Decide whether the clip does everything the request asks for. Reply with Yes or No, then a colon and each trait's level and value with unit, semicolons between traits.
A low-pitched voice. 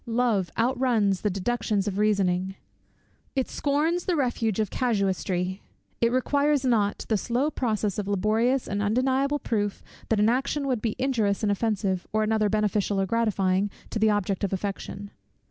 No: high, 215 Hz